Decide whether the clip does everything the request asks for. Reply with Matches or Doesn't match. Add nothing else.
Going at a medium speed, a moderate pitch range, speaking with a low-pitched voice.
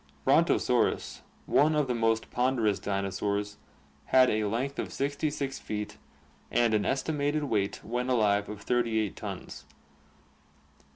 Doesn't match